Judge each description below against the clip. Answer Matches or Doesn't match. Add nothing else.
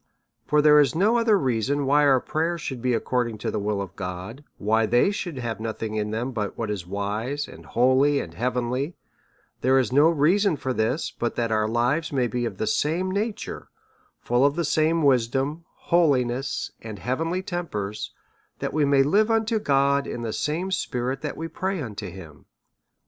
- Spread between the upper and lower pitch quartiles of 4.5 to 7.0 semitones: Matches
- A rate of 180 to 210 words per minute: Matches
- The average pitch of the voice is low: Matches